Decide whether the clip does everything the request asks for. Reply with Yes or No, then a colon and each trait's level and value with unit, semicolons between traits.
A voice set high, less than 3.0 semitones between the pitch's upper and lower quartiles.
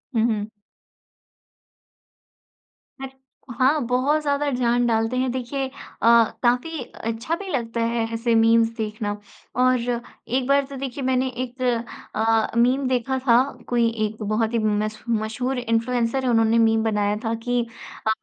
Yes: high, 240 Hz; narrow, 2.4 semitones